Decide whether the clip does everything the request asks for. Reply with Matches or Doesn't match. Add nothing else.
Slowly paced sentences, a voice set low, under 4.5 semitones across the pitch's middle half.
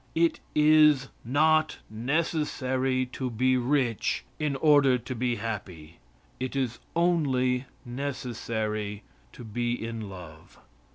Matches